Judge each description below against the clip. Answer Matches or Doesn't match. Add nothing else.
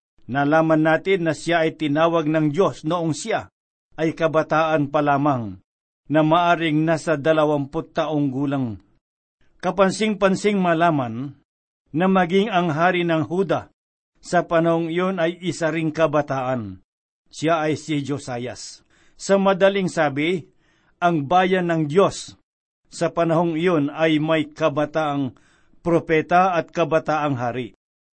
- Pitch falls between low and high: Matches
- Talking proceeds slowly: Doesn't match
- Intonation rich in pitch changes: Doesn't match